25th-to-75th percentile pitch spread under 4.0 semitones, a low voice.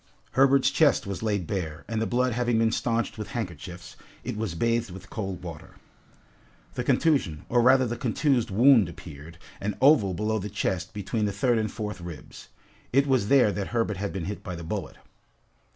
No: average, 4.5 semitones; low, 110 Hz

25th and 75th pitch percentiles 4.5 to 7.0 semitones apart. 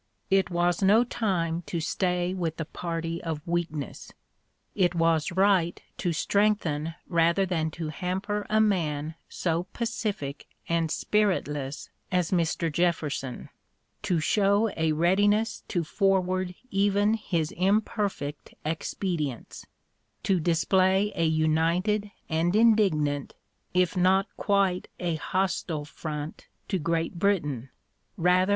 No: average, 3.3 semitones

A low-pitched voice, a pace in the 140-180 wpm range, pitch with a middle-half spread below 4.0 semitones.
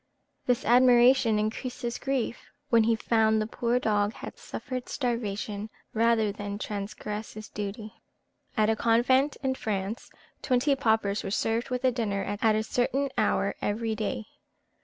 No: high, 225 Hz; average, 150 wpm; average, 2.7 semitones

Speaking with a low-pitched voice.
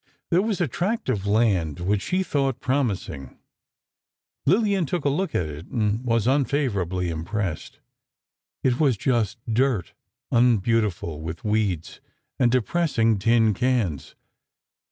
Yes: low, 115 Hz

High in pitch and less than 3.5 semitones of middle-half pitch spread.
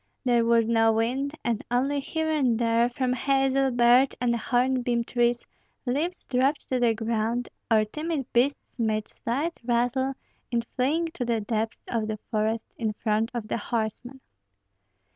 Yes: high, 240 Hz; average, 2.7 semitones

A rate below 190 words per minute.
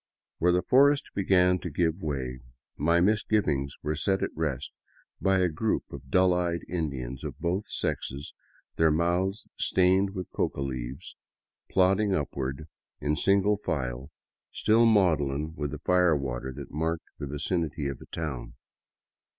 Yes: average, 145 wpm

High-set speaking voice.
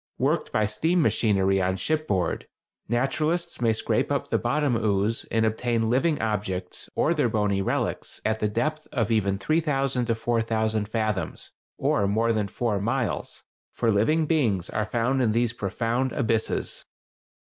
No: low, 115 Hz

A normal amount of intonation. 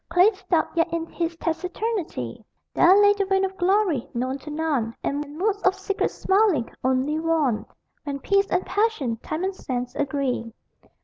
No: wide, 5.7 semitones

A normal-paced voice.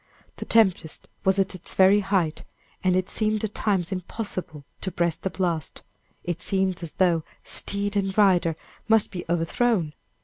Yes: average, 160 wpm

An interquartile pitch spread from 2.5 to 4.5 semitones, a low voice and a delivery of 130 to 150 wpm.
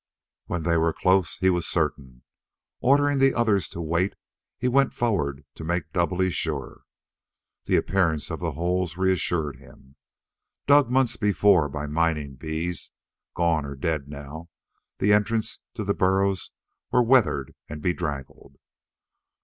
No: average, 4.9 semitones; very low, 85 Hz; average, 140 wpm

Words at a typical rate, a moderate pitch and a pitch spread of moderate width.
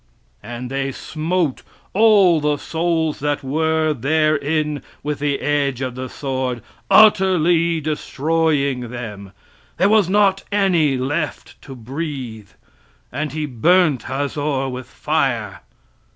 No: slow, 115 wpm; medium, 150 Hz; average, 3.6 semitones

